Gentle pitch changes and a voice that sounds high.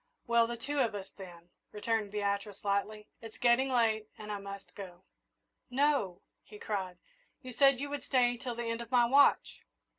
No: average, 3.6 semitones; high, 225 Hz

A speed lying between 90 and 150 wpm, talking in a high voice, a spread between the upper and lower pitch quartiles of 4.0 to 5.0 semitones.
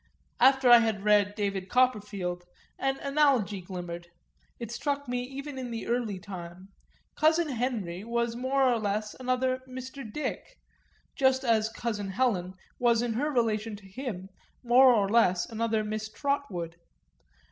Yes: average, 145 wpm; high, 230 Hz; average, 4.3 semitones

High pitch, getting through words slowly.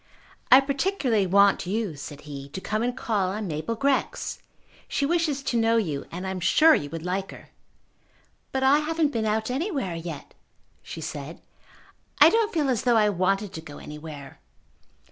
No: high, 210 Hz; average, 180 wpm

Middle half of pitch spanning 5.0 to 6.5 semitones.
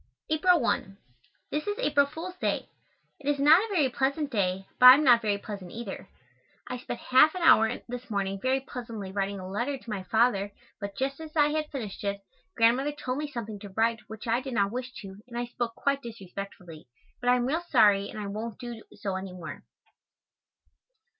Yes: wide, 5.6 semitones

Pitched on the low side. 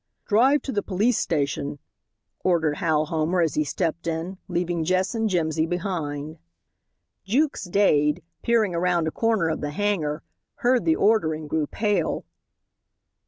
No: medium, 175 Hz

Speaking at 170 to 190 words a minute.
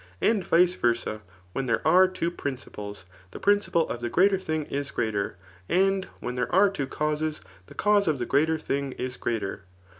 Yes: average, 180 wpm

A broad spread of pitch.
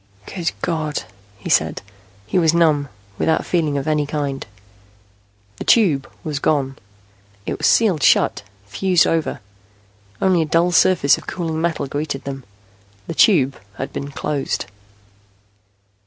No: average, 3.2 semitones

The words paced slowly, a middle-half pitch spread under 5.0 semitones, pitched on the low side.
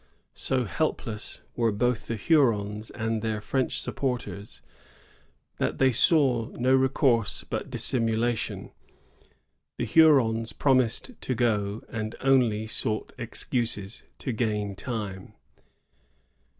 Yes: slow, 105 wpm; average, 3.0 semitones; low, 115 Hz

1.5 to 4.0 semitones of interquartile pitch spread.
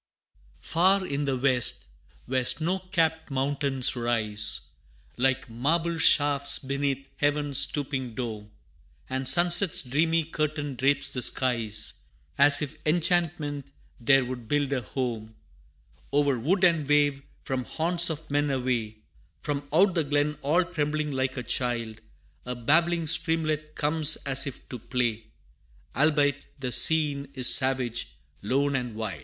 Yes: average, 3.5 semitones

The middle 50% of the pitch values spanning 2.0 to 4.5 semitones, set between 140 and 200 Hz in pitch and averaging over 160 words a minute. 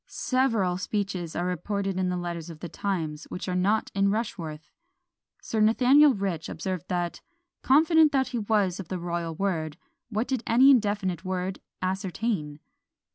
No: average, 4.0 semitones; high, 190 Hz; average, 155 wpm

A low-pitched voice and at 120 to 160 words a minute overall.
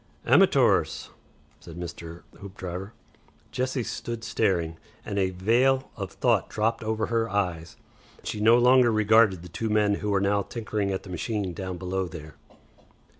Yes: low, 100 Hz; average, 150 wpm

